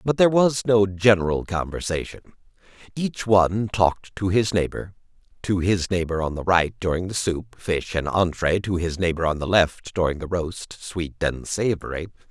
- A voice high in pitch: No, very low, 95 Hz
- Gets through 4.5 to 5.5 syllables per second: Yes, 4.9 syllables/s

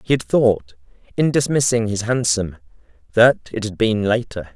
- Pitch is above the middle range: No, low, 110 Hz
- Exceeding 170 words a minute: No, average, 160 wpm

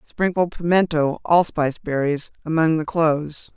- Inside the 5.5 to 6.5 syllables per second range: No, 4.7 syllables/s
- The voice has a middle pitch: Yes, medium, 160 Hz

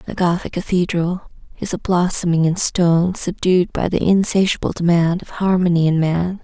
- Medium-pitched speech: Yes, medium, 175 Hz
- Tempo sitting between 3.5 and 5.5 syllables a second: Yes, 5.0 syllables/s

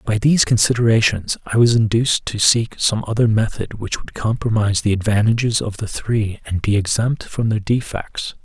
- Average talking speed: Yes, average, 180 wpm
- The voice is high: No, low, 110 Hz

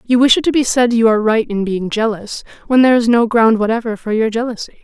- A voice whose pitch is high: Yes, high, 225 Hz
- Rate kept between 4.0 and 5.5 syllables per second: No, 6.3 syllables/s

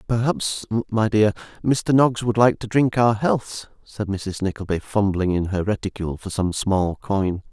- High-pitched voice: No, low, 105 Hz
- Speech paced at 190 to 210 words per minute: No, average, 175 wpm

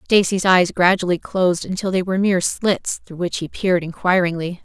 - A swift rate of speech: No, average, 180 wpm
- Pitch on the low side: No, medium, 180 Hz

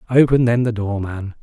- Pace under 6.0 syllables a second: Yes, 5.1 syllables/s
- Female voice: No, male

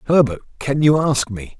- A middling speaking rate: Yes, average, 190 wpm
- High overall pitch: No, low, 130 Hz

